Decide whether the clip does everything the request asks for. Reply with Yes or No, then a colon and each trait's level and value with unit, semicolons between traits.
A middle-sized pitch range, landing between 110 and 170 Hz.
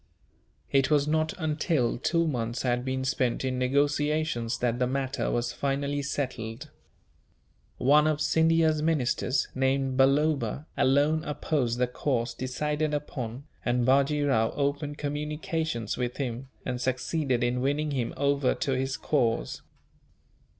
Yes: average, 3.0 semitones; low, 135 Hz